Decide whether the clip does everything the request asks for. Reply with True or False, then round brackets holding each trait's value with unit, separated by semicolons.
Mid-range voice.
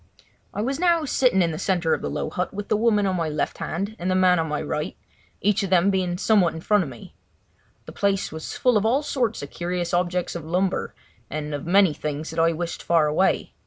True (180 Hz)